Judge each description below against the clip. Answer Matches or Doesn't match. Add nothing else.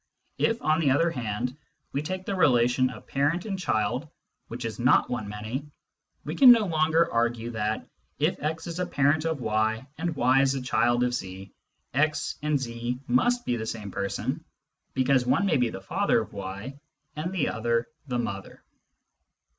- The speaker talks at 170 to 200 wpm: Matches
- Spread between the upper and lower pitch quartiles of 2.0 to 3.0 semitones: Doesn't match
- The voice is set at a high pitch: Doesn't match